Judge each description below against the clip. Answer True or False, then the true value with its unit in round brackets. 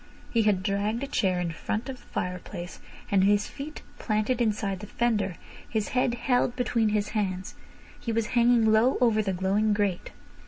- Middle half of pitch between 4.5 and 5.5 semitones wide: False (3.3 semitones)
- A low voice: False (215 Hz)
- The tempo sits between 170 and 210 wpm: True (180 wpm)